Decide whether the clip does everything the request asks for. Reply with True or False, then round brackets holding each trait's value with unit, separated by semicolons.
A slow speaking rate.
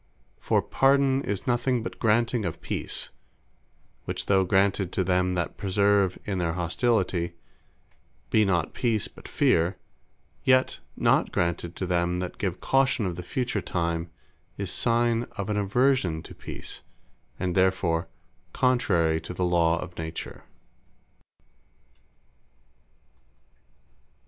True (125 wpm)